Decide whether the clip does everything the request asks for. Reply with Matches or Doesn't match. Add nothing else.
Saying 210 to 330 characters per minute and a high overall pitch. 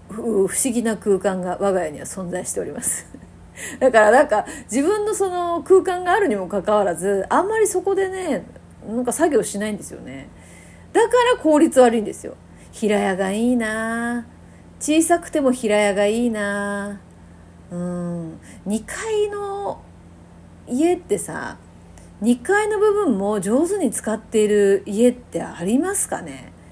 Matches